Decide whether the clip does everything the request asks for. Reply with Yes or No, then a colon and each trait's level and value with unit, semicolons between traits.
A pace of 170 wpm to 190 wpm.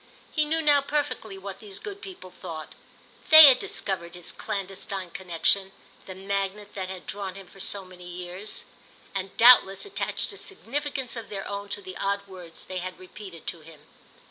Yes: average, 175 wpm